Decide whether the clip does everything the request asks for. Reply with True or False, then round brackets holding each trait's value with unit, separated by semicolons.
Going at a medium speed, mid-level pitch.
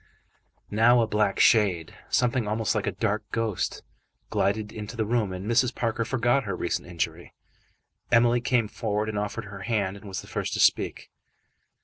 False (170 wpm; 110 Hz)